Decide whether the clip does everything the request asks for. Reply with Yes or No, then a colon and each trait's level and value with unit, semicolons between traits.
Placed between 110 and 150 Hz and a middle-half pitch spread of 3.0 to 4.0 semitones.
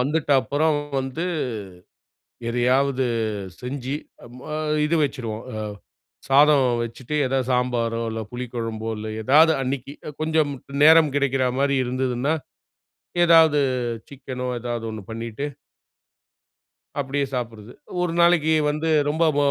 Yes: low, 135 Hz; average, 3.4 semitones